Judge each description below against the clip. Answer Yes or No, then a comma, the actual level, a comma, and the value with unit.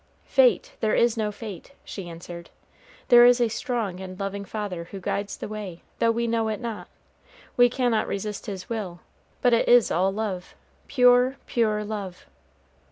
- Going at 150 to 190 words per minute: Yes, average, 165 wpm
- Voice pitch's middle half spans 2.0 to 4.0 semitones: Yes, average, 3.5 semitones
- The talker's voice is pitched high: Yes, high, 215 Hz